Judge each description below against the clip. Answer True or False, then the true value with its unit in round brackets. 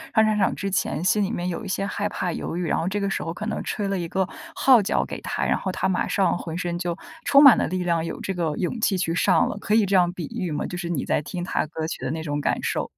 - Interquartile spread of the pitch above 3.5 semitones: False (2.8 semitones)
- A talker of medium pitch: True (180 Hz)